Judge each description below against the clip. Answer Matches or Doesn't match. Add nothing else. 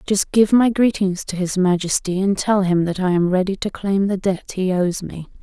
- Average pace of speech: Doesn't match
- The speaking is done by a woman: Matches